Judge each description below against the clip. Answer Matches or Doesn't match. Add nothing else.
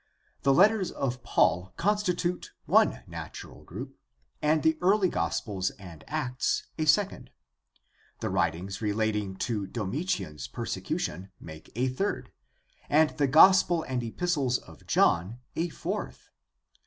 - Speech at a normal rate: Doesn't match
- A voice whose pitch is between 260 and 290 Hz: Doesn't match